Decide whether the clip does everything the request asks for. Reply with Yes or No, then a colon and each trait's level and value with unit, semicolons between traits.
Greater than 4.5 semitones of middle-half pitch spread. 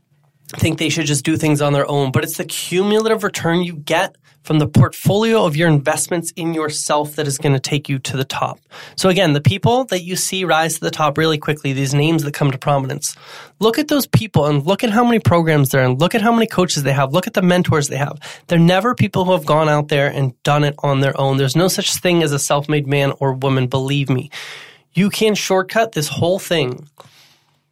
No: average, 4.1 semitones